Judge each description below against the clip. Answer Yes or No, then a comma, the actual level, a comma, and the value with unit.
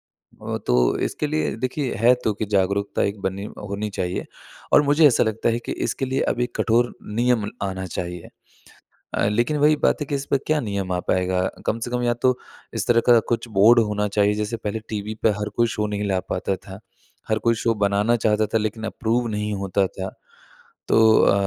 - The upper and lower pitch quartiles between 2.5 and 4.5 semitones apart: Yes, average, 3.2 semitones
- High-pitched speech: No, low, 110 Hz